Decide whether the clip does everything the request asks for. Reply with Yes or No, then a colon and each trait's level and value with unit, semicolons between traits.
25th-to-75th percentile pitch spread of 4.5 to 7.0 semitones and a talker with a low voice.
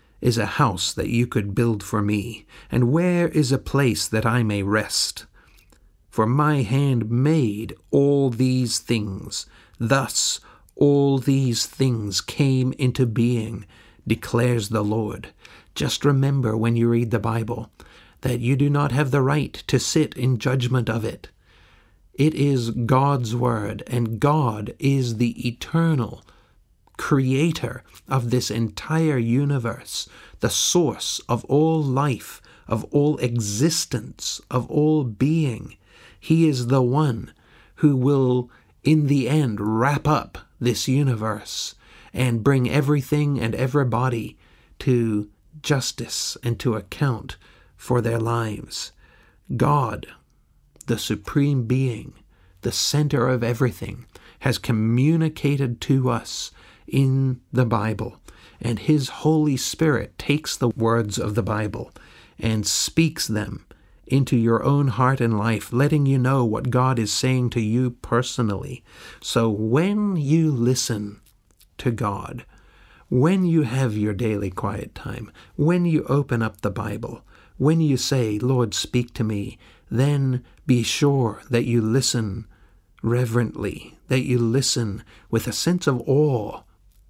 No: average, 3.9 semitones; low, 120 Hz